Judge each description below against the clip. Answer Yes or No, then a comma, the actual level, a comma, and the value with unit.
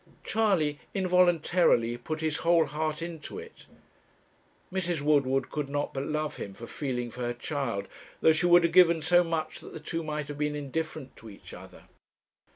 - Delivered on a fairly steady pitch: No, average, 3.5 semitones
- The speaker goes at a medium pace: Yes, average, 175 wpm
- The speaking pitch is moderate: Yes, medium, 155 Hz